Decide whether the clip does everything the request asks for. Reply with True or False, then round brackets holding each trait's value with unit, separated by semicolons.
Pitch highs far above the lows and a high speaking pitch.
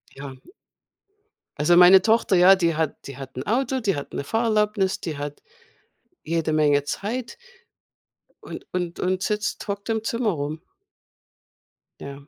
False (6.2 semitones; 180 Hz)